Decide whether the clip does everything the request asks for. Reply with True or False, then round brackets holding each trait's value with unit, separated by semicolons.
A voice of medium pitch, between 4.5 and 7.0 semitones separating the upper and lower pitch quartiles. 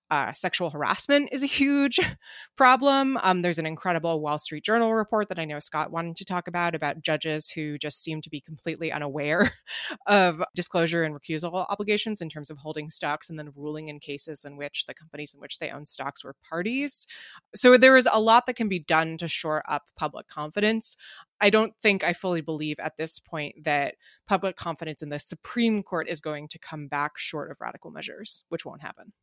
True (165 Hz; 5.3 semitones)